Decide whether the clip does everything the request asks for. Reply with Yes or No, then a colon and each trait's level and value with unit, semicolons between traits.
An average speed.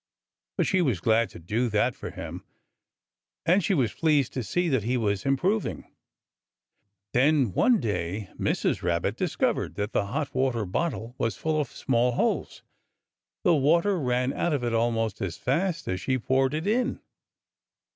Yes: average, 165 wpm